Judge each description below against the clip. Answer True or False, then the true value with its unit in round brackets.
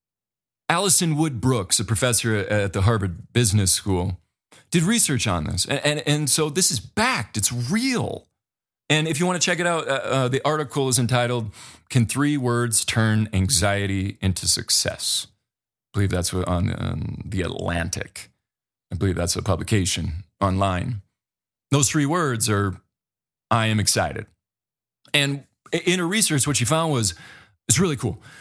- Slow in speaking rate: False (160 wpm)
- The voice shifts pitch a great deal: True (6.7 semitones)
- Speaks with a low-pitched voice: True (115 Hz)